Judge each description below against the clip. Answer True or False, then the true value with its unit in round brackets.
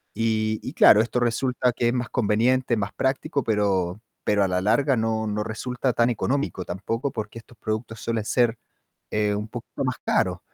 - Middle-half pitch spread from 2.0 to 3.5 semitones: True (2.7 semitones)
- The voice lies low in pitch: True (115 Hz)